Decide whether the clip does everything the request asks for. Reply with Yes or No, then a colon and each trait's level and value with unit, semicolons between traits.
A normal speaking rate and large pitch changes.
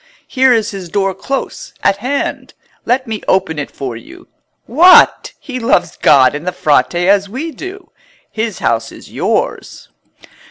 Yes: average, 155 wpm; wide, 6.8 semitones